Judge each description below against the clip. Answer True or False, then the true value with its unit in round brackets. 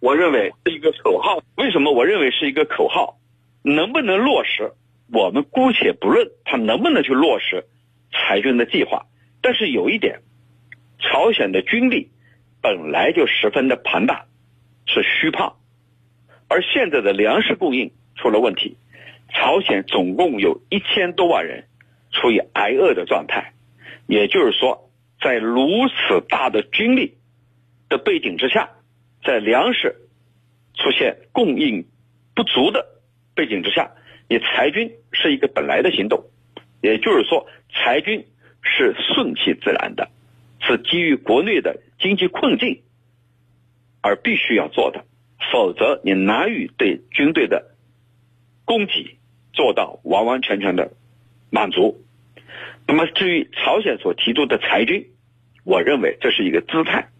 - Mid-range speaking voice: False (120 Hz)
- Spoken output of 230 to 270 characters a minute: False (210 characters per minute)